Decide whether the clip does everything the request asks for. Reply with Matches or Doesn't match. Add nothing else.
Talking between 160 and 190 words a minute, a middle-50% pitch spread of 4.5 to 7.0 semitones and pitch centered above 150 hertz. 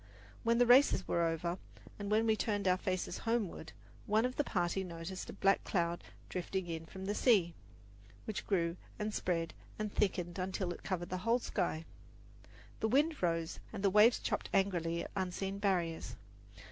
Doesn't match